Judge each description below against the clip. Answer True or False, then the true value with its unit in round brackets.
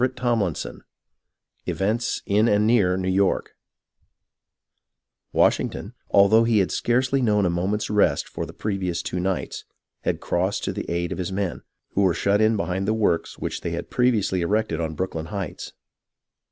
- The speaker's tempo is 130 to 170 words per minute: True (165 wpm)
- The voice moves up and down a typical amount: True (3.2 semitones)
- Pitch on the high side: False (100 Hz)